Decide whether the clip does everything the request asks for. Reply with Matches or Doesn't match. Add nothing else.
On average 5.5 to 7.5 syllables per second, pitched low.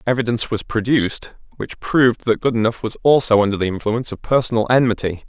Matches